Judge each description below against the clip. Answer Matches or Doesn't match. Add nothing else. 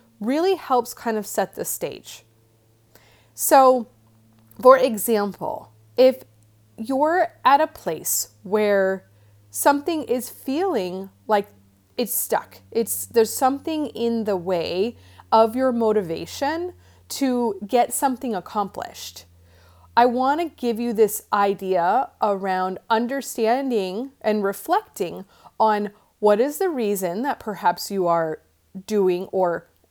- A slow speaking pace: Matches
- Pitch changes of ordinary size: Doesn't match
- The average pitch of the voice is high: Matches